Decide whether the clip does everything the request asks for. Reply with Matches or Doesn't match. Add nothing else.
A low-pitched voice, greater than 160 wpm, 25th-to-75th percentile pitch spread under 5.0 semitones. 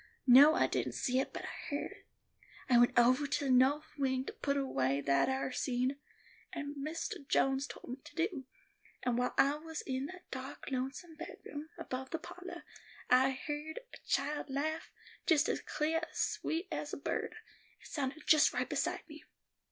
Doesn't match